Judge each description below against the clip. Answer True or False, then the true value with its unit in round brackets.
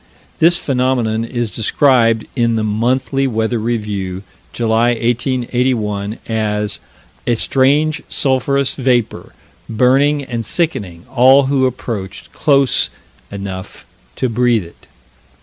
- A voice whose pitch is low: True (120 Hz)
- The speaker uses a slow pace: True (105 wpm)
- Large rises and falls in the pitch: False (3.2 semitones)